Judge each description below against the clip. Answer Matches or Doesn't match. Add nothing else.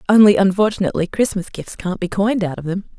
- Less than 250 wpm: Matches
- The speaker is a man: Doesn't match